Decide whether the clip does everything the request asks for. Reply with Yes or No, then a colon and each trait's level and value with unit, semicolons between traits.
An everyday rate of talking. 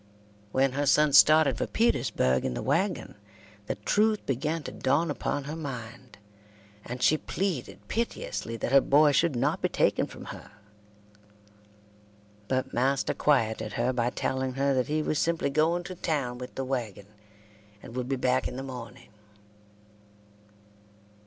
Yes: average, 150 wpm